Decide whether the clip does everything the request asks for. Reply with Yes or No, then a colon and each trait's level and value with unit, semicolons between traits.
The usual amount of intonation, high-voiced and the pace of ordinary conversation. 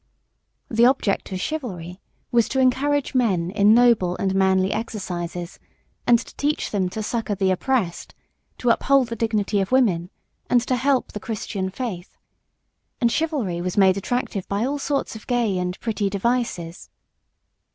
Yes: average, 4.7 semitones; high, 215 Hz; average, 155 wpm